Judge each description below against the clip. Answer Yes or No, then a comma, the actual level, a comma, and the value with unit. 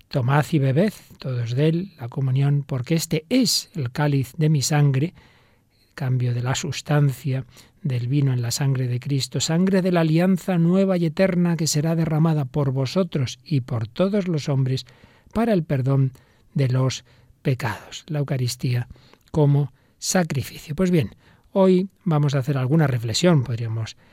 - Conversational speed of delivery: Yes, average, 160 wpm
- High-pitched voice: No, medium, 140 Hz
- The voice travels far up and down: No, average, 4.3 semitones